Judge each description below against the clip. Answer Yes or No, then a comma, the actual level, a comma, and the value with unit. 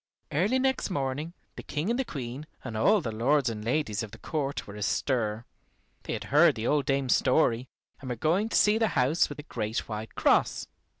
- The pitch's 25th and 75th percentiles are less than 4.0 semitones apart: No, wide, 5.4 semitones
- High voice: No, low, 135 Hz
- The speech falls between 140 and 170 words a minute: No, average, 200 wpm